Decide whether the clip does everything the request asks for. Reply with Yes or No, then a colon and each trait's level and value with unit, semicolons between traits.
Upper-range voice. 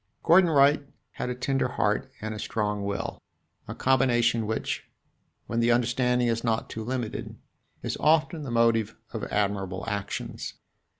No: low, 120 Hz